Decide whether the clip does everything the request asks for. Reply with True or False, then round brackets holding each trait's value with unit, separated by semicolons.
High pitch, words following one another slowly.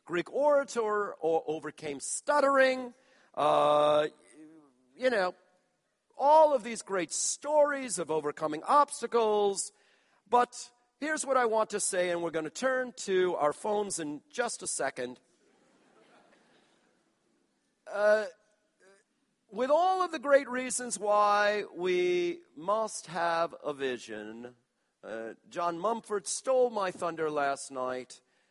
True (205 Hz; 120 wpm)